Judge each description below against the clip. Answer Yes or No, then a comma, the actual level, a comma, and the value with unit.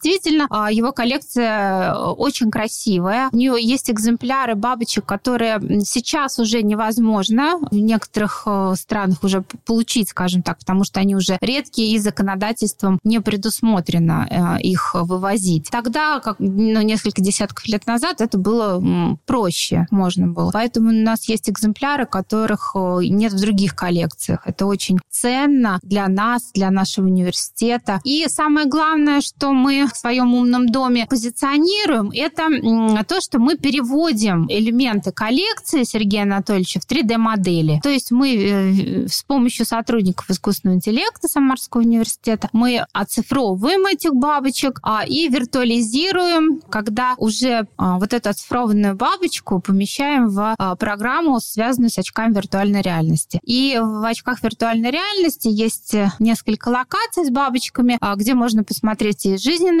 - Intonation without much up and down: No, average, 4.2 semitones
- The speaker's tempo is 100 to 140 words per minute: Yes, average, 130 wpm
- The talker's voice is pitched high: Yes, high, 225 Hz